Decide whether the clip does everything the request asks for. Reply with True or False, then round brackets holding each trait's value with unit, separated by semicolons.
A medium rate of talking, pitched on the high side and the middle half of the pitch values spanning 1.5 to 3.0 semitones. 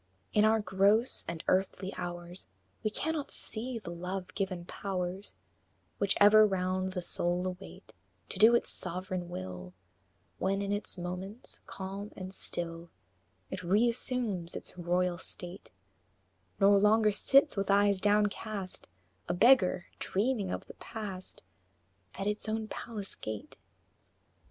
False (130 wpm; 195 Hz; 2.7 semitones)